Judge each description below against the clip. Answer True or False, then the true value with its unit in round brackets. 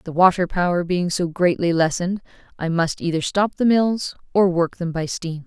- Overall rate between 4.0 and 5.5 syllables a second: True (5.0 syllables/s)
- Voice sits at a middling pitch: True (175 Hz)